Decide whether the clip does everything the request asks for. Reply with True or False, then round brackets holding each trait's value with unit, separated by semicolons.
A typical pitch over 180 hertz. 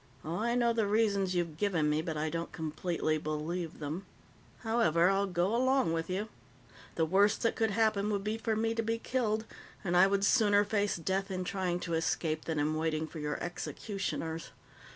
True (190 Hz)